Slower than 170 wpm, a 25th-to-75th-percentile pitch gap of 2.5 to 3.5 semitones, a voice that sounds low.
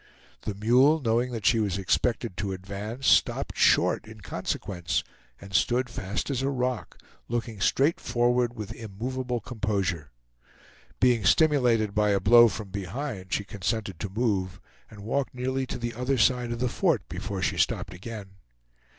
No: average, 160 wpm; average, 4.0 semitones; low, 115 Hz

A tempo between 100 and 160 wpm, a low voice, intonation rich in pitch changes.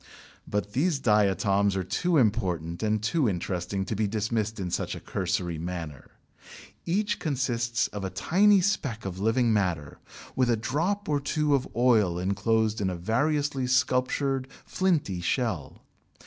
Yes: average, 150 wpm; low, 110 Hz; wide, 6.1 semitones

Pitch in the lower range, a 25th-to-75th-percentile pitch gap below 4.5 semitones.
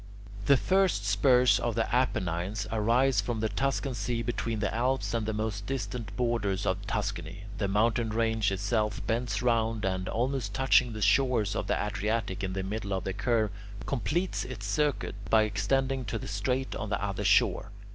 Yes: low, 110 Hz; average, 3.4 semitones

